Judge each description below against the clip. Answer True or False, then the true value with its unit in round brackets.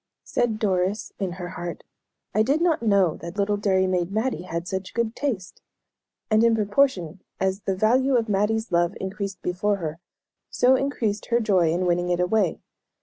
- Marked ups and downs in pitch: False (3.6 semitones)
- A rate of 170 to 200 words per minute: True (175 wpm)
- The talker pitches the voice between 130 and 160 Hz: False (200 Hz)